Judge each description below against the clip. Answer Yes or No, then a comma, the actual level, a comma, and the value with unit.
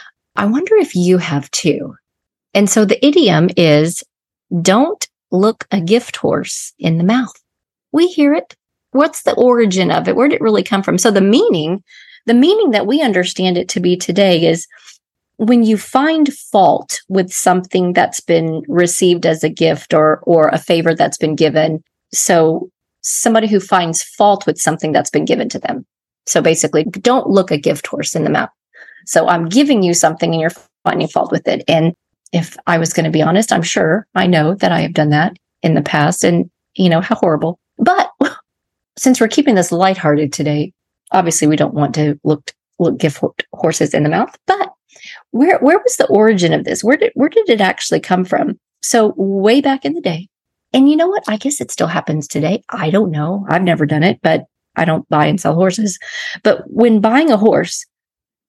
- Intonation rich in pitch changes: Yes, wide, 5.9 semitones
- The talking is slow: No, average, 200 wpm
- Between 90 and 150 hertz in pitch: No, medium, 185 Hz